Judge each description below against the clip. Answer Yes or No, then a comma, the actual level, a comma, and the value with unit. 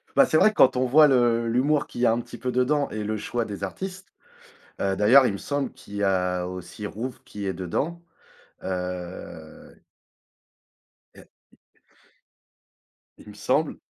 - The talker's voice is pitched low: Yes, low, 115 Hz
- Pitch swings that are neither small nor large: No, wide, 5.9 semitones